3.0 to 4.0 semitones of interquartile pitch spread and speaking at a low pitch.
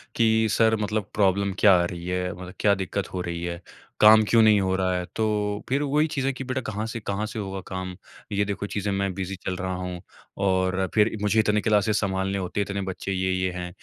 No: narrow, 2.4 semitones; low, 100 Hz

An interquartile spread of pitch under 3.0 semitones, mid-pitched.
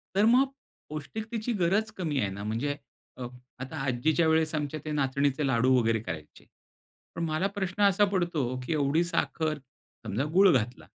No: wide, 5.6 semitones; medium, 155 Hz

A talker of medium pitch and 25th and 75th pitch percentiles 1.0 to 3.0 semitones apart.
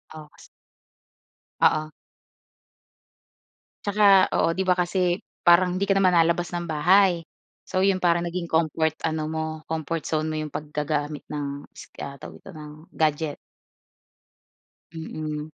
Yes: medium, 165 Hz; average, 2.7 semitones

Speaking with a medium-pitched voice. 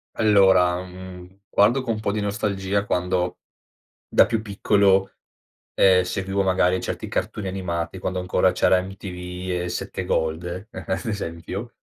No: very low, 95 Hz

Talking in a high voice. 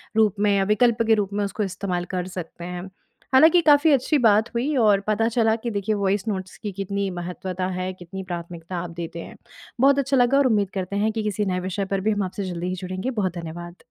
Yes: high, 200 Hz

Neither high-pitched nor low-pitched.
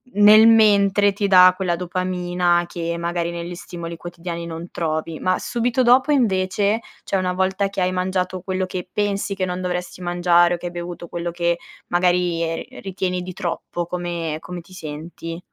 Yes: medium, 180 Hz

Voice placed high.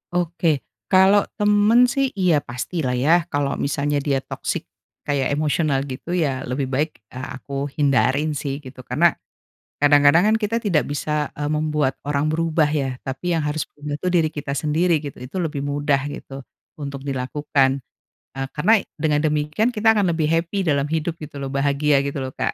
No: medium, 150 Hz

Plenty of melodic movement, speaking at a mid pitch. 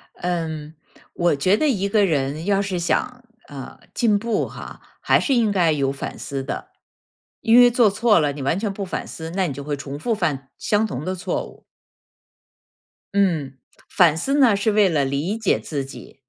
Yes: wide, 6.2 semitones; medium, 180 Hz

